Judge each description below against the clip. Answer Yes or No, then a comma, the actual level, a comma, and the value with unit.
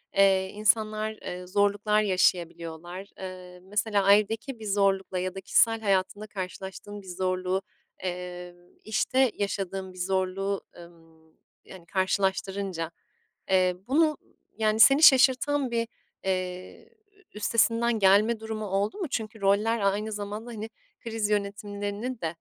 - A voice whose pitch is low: No, high, 200 Hz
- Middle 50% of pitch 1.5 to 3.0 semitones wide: Yes, average, 2.7 semitones